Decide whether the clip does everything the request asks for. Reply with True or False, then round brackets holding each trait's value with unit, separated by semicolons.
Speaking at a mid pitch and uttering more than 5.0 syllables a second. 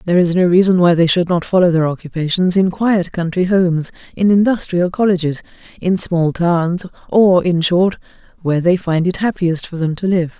True (175 Hz; 5.3 syllables/s)